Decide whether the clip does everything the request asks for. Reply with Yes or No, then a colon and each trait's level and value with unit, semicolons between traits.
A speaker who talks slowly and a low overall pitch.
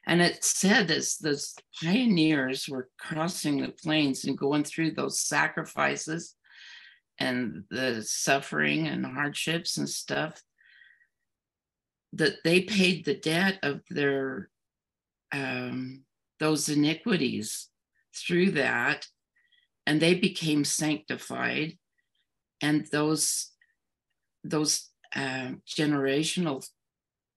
No: slow, 95 wpm; medium, 155 Hz